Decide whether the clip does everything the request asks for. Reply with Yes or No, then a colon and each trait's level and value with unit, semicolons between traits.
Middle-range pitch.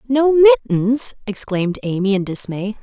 No: high, 225 Hz